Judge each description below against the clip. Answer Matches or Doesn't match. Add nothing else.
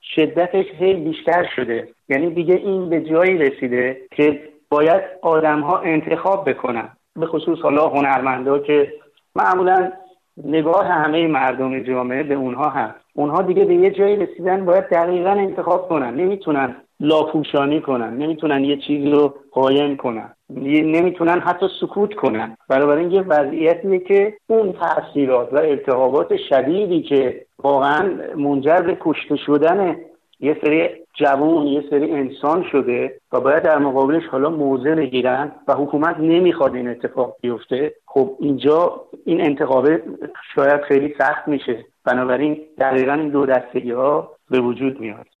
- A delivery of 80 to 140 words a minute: Matches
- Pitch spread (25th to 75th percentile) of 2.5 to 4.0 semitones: Doesn't match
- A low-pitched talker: Doesn't match